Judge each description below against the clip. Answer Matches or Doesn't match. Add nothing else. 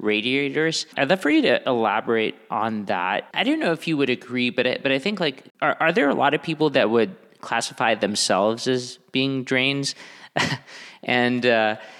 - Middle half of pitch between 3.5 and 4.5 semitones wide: Matches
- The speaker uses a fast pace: Doesn't match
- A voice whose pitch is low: Matches